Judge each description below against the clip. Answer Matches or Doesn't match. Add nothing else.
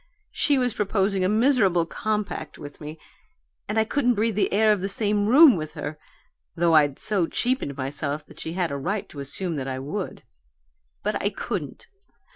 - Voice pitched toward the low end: Doesn't match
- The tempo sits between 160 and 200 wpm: Matches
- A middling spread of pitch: Doesn't match